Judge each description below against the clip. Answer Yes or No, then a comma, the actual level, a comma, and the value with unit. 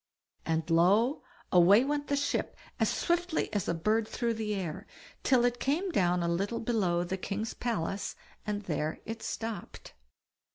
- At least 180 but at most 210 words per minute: No, average, 160 wpm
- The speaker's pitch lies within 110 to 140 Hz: No, high, 210 Hz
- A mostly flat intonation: No, wide, 5.4 semitones